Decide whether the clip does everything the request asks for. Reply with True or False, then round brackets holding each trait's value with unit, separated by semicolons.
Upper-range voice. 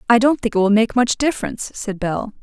True (225 Hz)